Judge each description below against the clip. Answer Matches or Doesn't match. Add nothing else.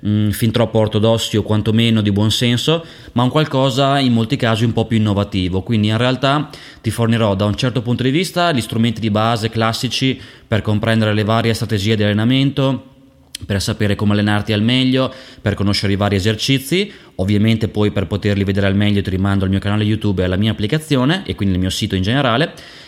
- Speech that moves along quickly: Matches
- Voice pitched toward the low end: Matches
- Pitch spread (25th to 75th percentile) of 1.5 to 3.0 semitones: Doesn't match